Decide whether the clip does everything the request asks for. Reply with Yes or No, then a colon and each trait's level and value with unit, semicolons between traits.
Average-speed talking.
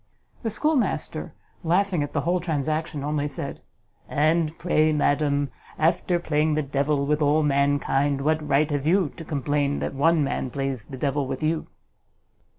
Yes: average, 155 wpm